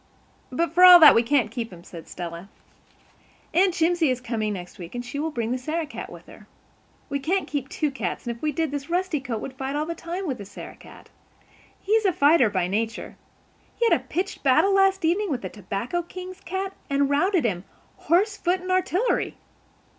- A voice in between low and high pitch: No, very high, 290 Hz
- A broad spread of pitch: Yes, wide, 7.3 semitones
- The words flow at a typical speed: No, fast, 210 wpm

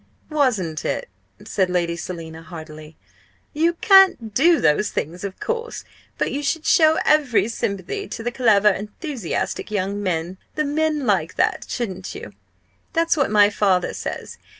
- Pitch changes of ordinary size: No, wide, 8.9 semitones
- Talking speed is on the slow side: No, average, 150 wpm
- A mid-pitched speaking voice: No, high, 210 Hz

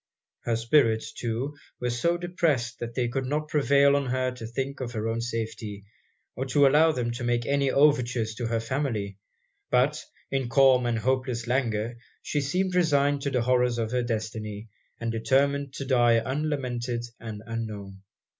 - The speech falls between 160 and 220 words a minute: Yes, average, 170 wpm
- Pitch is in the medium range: No, low, 125 Hz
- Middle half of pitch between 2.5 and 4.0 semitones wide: Yes, average, 3.3 semitones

